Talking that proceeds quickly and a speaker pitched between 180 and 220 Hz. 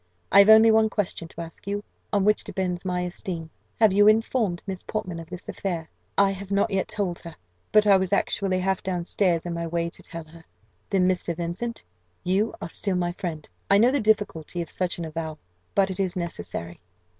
Yes: fast, 210 wpm; medium, 185 Hz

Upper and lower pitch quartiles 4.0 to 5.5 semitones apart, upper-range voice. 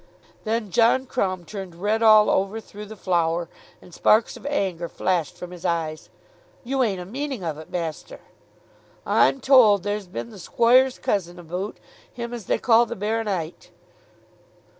Yes: average, 4.7 semitones; high, 205 Hz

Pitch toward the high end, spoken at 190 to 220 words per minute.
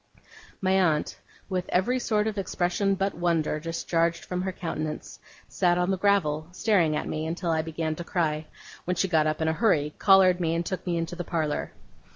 No: medium, 175 Hz; average, 200 wpm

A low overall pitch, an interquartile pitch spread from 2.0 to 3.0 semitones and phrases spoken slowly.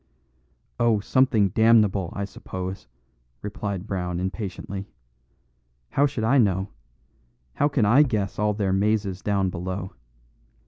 Yes: low, 100 Hz; average, 2.7 semitones; slow, 120 wpm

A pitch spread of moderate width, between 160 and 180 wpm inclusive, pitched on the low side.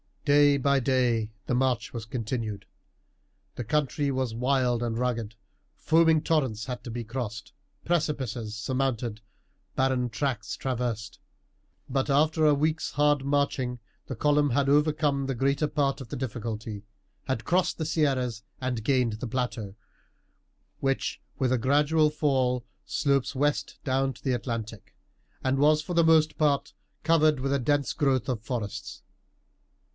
No: average, 3.5 semitones; average, 145 wpm; low, 130 Hz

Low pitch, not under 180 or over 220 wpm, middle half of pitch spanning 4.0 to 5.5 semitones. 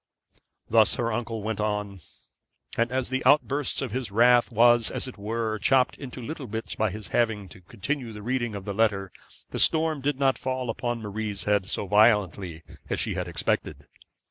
No: low, 115 Hz; average, 185 wpm; average, 3.6 semitones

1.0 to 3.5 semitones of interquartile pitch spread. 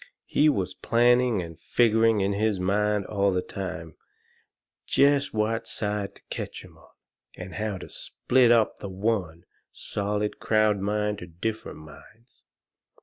Yes: average, 2.9 semitones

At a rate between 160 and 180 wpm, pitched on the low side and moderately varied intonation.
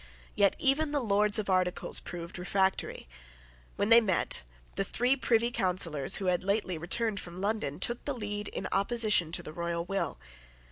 No: average, 170 wpm; high, 200 Hz; average, 4.1 semitones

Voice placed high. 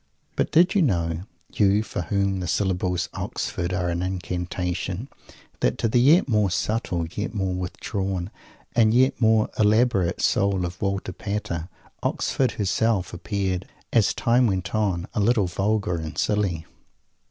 No: low, 100 Hz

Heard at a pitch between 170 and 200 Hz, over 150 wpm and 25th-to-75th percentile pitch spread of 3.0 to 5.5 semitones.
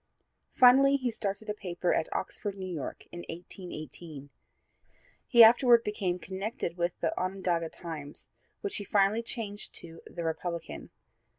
No: high, 190 Hz; slow, 135 wpm; average, 4.3 semitones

